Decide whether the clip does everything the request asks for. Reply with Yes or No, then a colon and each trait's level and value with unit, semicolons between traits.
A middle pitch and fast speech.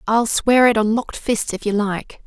No: high, 220 Hz; fast, 240 wpm